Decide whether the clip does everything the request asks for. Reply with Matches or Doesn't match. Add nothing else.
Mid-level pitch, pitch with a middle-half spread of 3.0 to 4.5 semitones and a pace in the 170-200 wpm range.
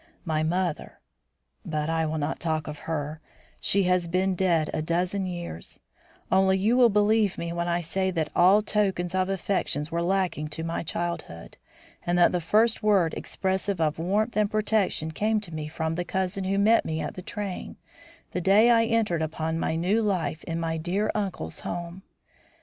Matches